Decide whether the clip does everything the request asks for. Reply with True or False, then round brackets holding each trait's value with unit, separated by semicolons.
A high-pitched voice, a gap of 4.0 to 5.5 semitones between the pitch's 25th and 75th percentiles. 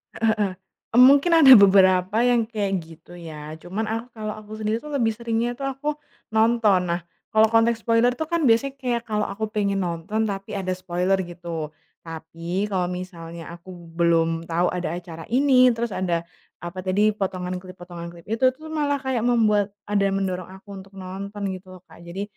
True (200 Hz; 4.4 semitones)